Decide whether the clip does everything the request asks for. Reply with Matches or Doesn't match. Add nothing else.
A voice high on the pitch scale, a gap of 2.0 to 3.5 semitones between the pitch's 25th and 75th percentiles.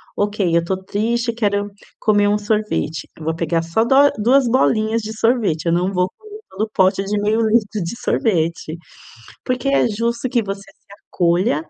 Doesn't match